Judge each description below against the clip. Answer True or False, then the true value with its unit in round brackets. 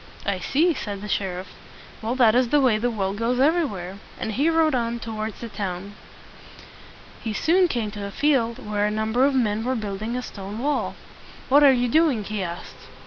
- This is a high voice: True (230 Hz)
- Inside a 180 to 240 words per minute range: True (200 wpm)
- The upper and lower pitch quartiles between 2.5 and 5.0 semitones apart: True (4.1 semitones)